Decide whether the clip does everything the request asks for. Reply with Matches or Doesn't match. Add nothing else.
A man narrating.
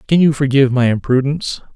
Matches